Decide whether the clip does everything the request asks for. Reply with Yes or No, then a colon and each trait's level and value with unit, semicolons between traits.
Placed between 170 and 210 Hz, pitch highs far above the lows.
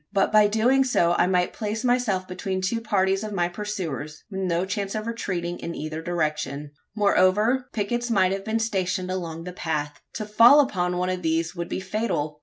No: high, 190 Hz; average, 3.7 semitones